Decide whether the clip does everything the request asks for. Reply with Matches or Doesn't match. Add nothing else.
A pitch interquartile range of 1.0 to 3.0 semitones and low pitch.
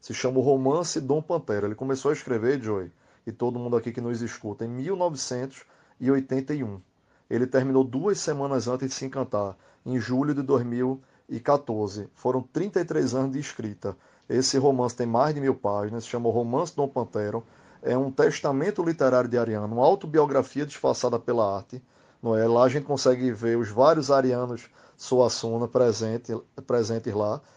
Matches